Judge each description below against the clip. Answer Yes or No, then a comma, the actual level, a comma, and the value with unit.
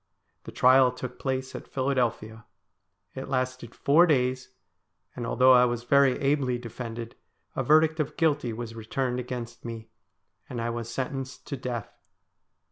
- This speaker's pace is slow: No, average, 145 wpm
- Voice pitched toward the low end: Yes, low, 125 Hz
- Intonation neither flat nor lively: No, narrow, 2.1 semitones